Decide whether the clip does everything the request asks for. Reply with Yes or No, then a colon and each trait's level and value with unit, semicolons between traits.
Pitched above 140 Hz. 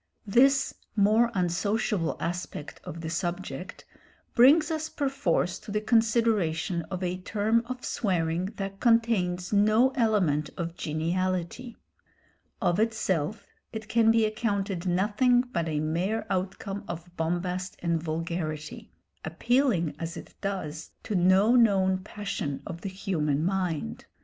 Yes: high, 190 Hz